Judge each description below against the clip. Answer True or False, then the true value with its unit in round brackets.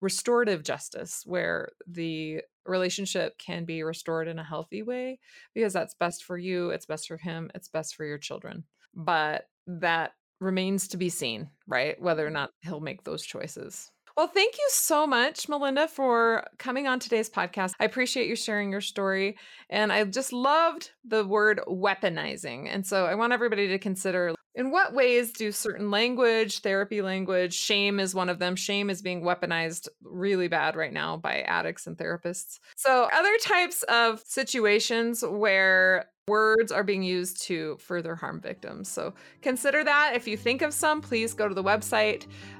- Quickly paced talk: False (175 wpm)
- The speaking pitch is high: True (205 Hz)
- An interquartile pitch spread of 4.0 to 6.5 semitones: True (5.0 semitones)